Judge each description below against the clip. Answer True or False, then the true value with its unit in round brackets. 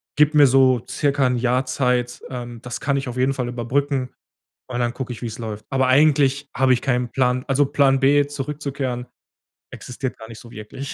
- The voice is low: True (130 Hz)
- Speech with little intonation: True (2.2 semitones)